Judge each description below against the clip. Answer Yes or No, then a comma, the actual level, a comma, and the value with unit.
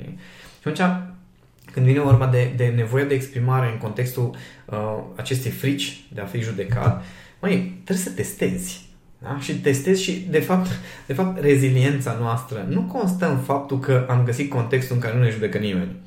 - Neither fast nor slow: No, fast, 175 wpm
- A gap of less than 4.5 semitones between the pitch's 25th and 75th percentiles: Yes, average, 3.7 semitones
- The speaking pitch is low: Yes, low, 130 Hz